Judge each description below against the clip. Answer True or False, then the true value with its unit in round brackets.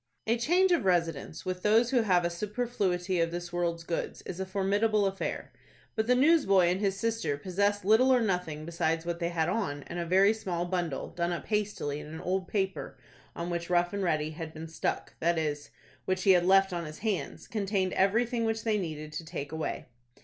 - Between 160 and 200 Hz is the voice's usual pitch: True (185 Hz)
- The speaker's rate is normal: False (210 wpm)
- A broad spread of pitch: False (3.7 semitones)